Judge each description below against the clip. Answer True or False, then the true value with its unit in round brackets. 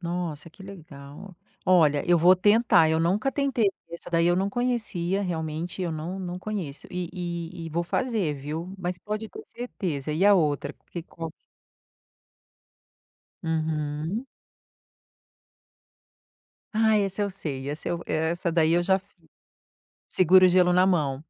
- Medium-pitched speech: True (175 Hz)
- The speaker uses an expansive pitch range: False (3.4 semitones)